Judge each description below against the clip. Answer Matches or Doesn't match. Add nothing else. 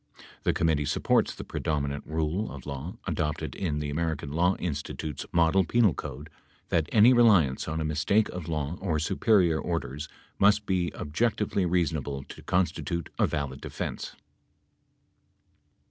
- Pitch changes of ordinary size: Matches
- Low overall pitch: Matches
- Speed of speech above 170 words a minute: Doesn't match